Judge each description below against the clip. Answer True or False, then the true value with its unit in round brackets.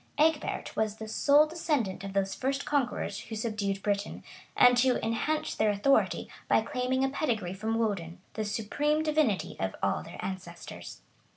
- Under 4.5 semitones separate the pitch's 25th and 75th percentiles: False (5.5 semitones)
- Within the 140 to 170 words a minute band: True (155 wpm)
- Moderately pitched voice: False (225 Hz)